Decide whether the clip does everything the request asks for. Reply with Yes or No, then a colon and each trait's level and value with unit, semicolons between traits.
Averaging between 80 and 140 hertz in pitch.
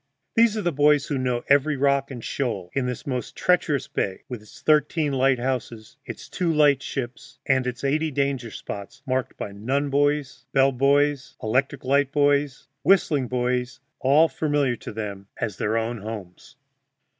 Yes: low, 135 Hz